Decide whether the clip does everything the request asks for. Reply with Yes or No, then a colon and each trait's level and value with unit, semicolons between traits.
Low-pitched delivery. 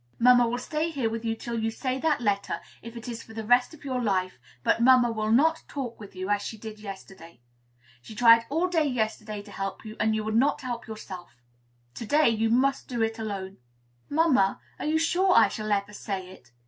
No: high, 225 Hz